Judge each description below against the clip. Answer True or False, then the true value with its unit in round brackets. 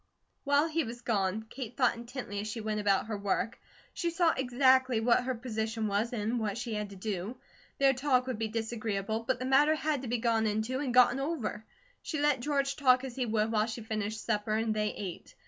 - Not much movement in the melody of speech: False (3.3 semitones)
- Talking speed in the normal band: False (215 wpm)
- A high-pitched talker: True (235 Hz)